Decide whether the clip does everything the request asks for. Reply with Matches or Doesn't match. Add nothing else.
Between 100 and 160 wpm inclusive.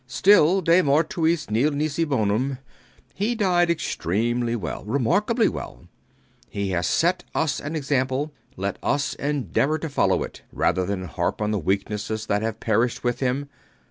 Matches